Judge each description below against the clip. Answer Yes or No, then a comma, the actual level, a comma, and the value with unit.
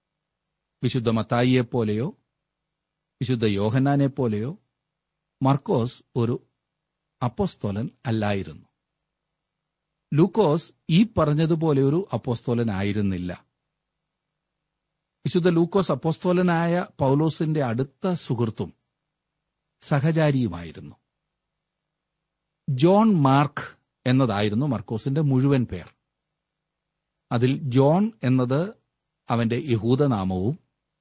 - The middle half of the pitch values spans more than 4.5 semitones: Yes, average, 5.3 semitones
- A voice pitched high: No, medium, 140 Hz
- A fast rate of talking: No, slow, 60 wpm